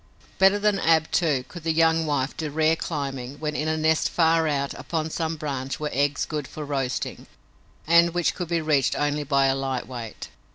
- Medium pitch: Yes, medium, 155 Hz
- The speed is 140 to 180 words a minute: No, average, 200 wpm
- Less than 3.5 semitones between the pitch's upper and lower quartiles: Yes, average, 2.8 semitones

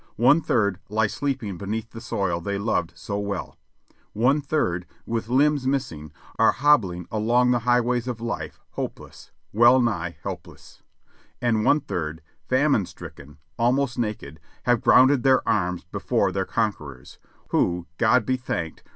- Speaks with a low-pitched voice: Yes, low, 110 Hz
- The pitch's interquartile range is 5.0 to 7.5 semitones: Yes, wide, 5.5 semitones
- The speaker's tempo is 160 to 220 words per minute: No, average, 145 wpm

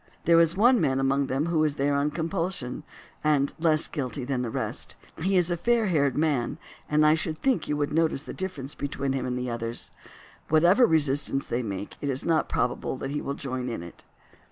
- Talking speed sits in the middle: No, fast, 215 wpm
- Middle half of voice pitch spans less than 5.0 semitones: Yes, average, 3.6 semitones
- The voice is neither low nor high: Yes, medium, 145 Hz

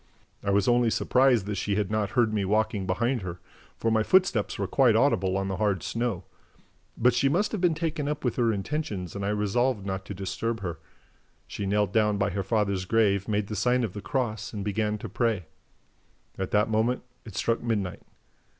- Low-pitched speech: Yes, low, 105 Hz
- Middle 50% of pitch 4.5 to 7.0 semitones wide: No, average, 3.4 semitones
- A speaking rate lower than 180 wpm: No, fast, 205 wpm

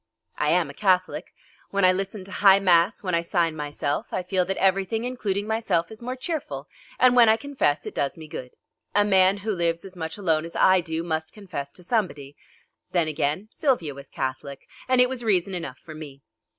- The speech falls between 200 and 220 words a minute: Yes, fast, 205 wpm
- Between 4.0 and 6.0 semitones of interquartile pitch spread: Yes, average, 4.5 semitones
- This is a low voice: No, medium, 185 Hz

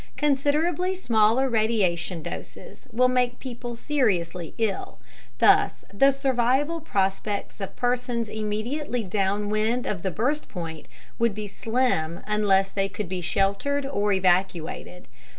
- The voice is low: No, high, 215 Hz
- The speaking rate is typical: No, slow, 120 wpm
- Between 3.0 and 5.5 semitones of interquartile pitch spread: Yes, average, 4.6 semitones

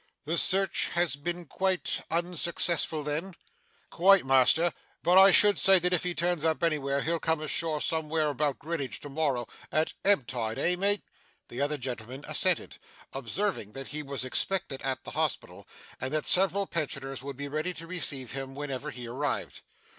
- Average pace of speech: Yes, average, 170 wpm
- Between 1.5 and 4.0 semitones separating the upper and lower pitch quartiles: No, average, 4.4 semitones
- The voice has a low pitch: No, medium, 155 Hz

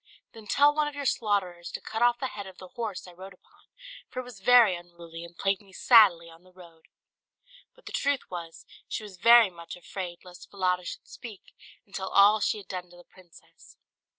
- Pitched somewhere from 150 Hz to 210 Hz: Yes, high, 190 Hz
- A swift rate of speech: Yes, fast, 215 wpm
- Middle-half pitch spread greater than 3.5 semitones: Yes, average, 4.1 semitones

